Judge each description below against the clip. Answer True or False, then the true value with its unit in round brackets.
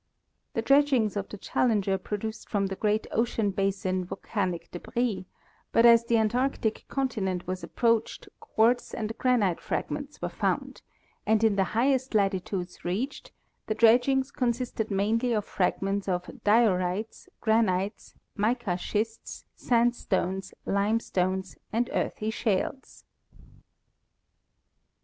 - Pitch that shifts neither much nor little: True (3.4 semitones)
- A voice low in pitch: False (215 Hz)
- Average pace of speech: False (115 wpm)